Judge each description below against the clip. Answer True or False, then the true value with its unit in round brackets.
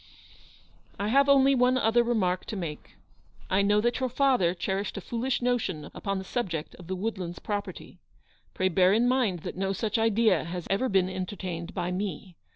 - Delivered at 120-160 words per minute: False (185 wpm)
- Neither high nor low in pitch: False (200 Hz)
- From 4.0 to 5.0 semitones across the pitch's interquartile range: True (4.6 semitones)